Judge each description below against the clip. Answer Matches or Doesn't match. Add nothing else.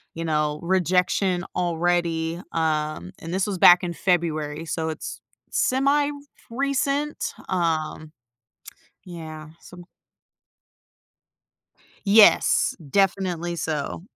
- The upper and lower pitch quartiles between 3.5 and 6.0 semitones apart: Doesn't match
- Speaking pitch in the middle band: Matches